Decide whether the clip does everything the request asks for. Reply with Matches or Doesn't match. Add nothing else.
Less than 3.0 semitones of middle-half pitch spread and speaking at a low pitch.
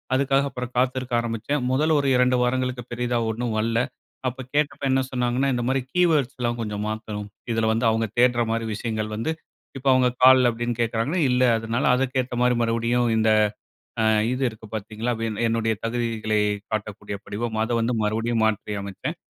Matches